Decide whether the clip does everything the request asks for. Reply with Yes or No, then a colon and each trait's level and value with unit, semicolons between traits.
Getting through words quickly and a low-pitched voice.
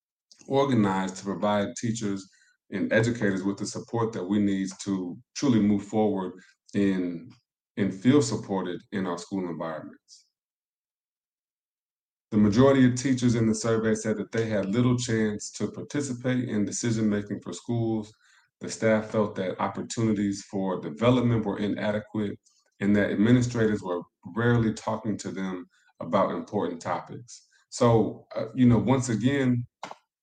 No: average, 140 wpm; low, 110 Hz